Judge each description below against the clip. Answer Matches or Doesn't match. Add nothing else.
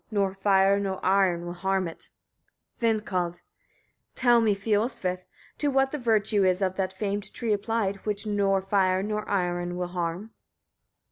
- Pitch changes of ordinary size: Doesn't match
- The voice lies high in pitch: Matches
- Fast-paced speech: Doesn't match